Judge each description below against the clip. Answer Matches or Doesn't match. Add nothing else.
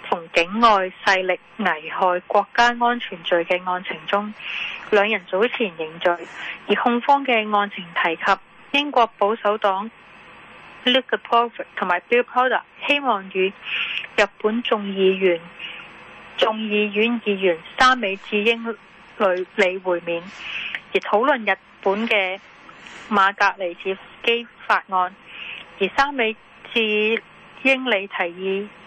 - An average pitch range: Matches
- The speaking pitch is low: Doesn't match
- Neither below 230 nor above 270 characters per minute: Doesn't match